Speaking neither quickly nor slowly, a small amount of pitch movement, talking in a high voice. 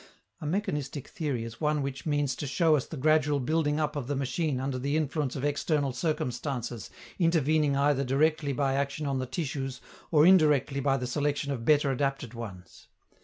No: average, 180 wpm; narrow, 2.3 semitones; medium, 140 Hz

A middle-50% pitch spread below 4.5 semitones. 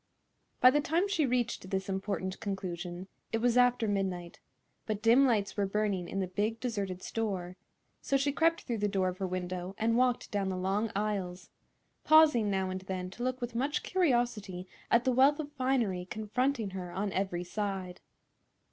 No: average, 4.8 semitones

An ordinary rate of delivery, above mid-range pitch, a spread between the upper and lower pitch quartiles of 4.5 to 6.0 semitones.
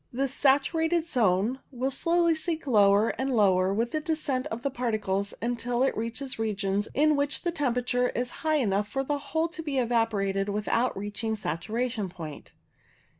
Yes: average, 165 wpm; high, 245 Hz; average, 5.2 semitones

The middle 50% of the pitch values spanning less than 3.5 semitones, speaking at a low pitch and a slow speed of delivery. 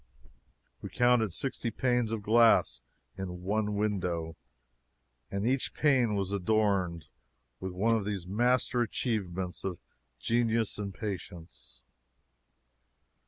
No: average, 4.1 semitones; low, 105 Hz; slow, 110 wpm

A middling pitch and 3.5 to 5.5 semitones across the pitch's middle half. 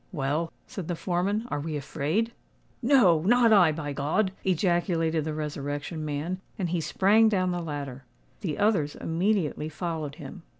Yes: medium, 165 Hz; average, 4.3 semitones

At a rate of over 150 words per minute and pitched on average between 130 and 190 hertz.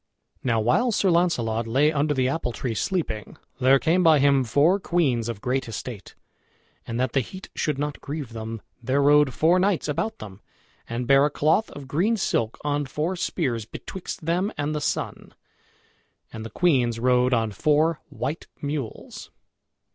Yes: average, 170 wpm; medium, 140 Hz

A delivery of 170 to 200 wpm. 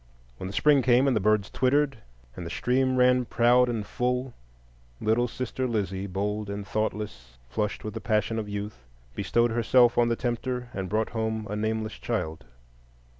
Yes: average, 175 wpm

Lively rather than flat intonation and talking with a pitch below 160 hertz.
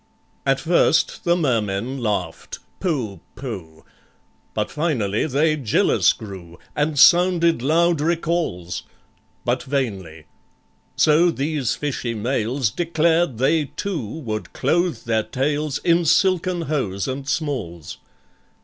Yes: wide, 7.1 semitones; medium, 140 Hz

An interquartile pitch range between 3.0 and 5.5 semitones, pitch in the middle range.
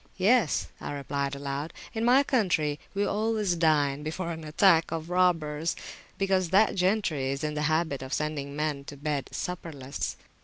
Yes: average, 4.4 semitones; medium, 160 Hz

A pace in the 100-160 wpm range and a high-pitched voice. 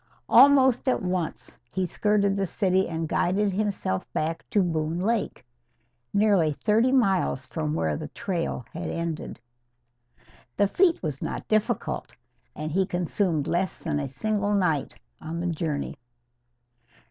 No: slow, 135 wpm; medium, 180 Hz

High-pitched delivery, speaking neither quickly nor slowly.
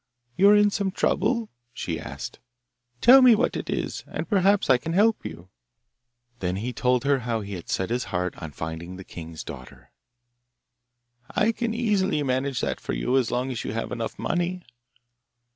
No: low, 130 Hz; average, 180 wpm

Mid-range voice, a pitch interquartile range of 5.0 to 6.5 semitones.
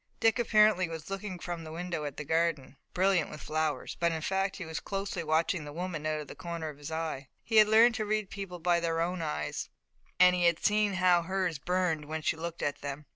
No: medium, 170 Hz; average, 3.2 semitones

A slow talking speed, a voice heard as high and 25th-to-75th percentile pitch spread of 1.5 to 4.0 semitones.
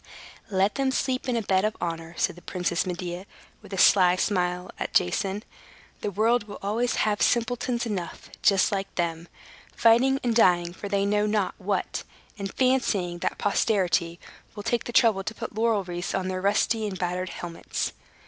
No: average, 175 wpm; high, 200 Hz; average, 3.6 semitones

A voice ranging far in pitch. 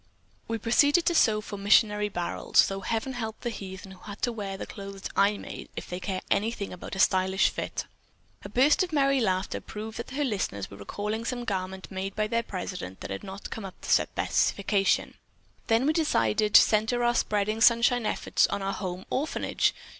No: average, 3.4 semitones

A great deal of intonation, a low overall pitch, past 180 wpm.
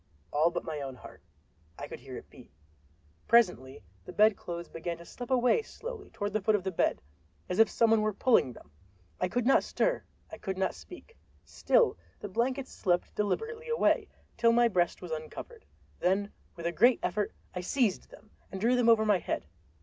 No: wide, 5.7 semitones; high, 210 Hz; average, 190 wpm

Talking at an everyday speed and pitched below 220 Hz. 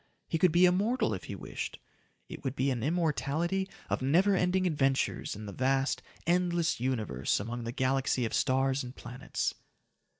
Yes: average, 165 wpm; low, 135 Hz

